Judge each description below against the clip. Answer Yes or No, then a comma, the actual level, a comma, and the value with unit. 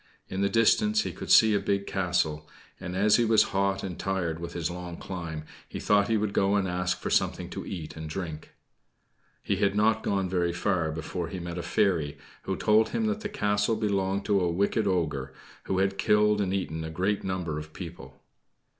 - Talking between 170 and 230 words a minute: Yes, fast, 205 wpm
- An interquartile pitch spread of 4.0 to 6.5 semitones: No, average, 3.2 semitones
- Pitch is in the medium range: No, very low, 95 Hz